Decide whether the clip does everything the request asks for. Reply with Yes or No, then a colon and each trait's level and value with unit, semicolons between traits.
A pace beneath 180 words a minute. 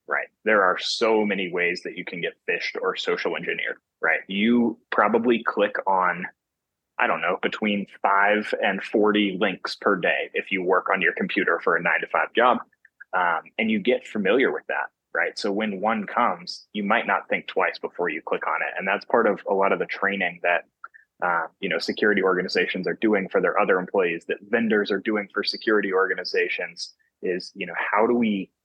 No: fast, 205 wpm